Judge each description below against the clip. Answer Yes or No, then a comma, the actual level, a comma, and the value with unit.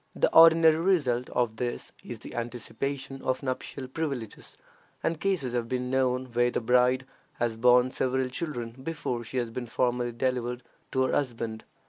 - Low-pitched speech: Yes, low, 125 Hz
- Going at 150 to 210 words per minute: Yes, average, 160 wpm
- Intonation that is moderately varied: No, narrow, 1.9 semitones